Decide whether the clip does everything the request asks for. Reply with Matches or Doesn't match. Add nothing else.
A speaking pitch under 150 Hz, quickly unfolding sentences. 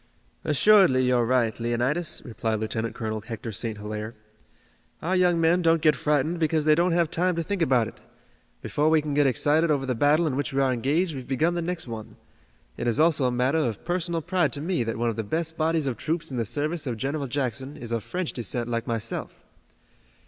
Matches